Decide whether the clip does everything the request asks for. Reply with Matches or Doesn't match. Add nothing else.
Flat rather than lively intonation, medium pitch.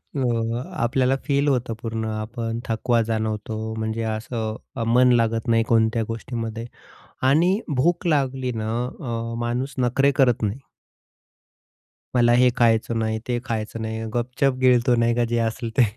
Doesn't match